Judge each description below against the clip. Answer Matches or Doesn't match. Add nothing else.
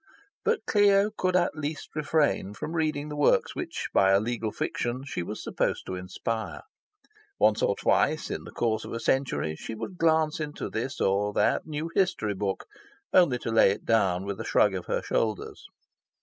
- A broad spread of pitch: Matches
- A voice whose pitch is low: Matches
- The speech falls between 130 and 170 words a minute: Doesn't match